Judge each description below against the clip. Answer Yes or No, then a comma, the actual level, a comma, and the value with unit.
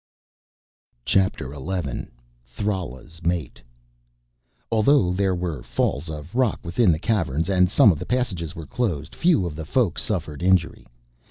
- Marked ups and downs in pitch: No, average, 4.3 semitones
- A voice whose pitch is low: Yes, very low, 90 Hz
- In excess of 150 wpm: No, average, 140 wpm